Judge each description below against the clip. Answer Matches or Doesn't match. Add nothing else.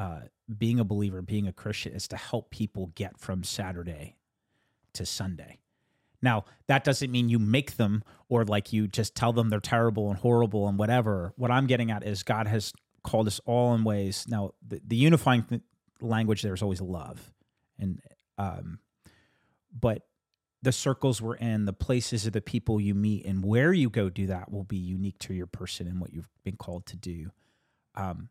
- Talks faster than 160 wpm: Matches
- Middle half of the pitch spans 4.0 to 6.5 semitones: Doesn't match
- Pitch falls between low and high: Doesn't match